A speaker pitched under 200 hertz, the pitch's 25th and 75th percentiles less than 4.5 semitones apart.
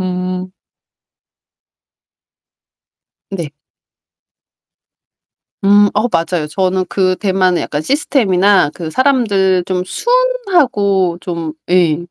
Yes: medium, 185 Hz; narrow, 2.5 semitones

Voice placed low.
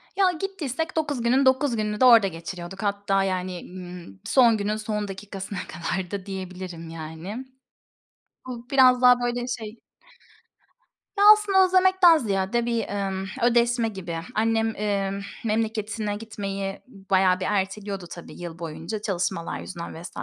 No: high, 210 Hz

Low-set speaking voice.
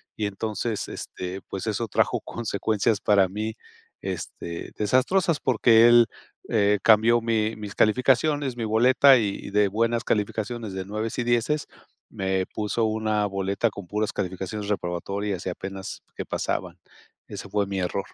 Yes: low, 105 Hz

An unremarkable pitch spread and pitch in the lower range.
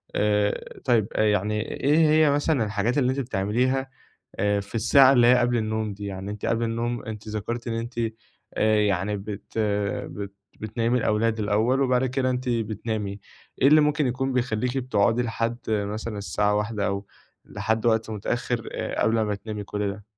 Yes: average, 3.0 semitones; low, 110 Hz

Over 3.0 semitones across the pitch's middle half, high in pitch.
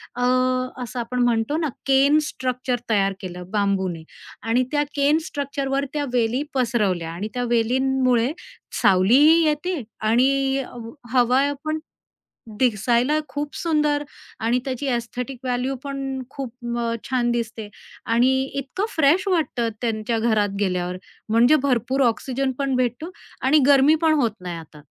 Yes: average, 3.5 semitones; very high, 250 Hz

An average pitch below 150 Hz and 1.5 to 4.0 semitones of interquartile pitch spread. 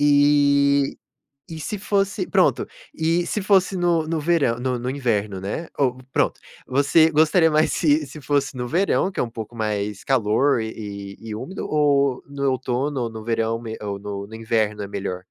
No: low, 135 Hz; wide, 5.5 semitones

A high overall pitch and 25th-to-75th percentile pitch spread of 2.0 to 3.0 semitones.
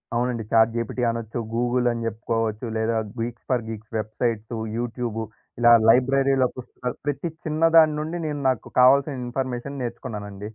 No: low, 120 Hz; narrow, 2.6 semitones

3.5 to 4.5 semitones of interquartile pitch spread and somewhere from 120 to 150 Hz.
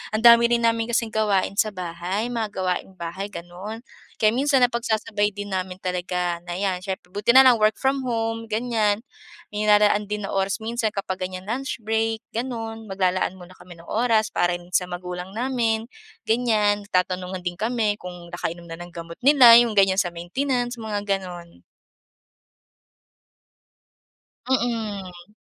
No: average, 3.9 semitones; high, 210 Hz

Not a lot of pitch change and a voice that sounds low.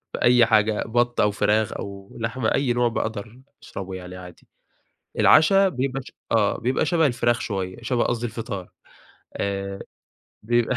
No: average, 3.5 semitones; low, 115 Hz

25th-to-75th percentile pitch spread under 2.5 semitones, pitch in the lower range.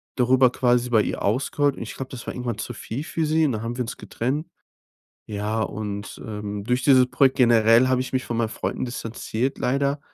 No: average, 2.8 semitones; low, 125 Hz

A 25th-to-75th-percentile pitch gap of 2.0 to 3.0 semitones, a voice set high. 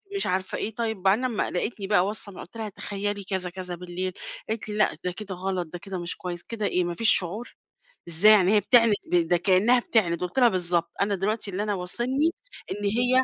No: average, 3.4 semitones; high, 195 Hz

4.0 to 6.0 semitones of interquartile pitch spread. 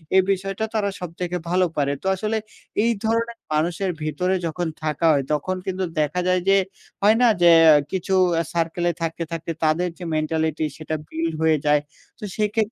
No: average, 3.4 semitones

